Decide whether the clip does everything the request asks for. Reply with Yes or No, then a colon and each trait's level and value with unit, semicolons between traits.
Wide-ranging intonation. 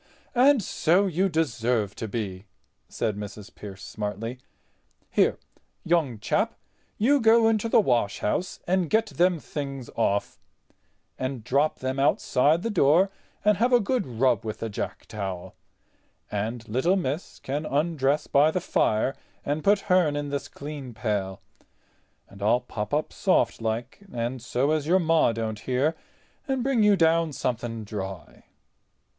Yes: wide, 7.5 semitones